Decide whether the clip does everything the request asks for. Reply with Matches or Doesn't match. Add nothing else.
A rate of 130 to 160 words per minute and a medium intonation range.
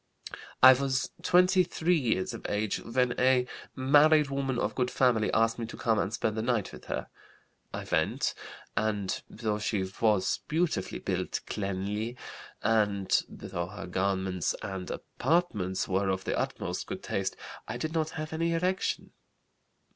Doesn't match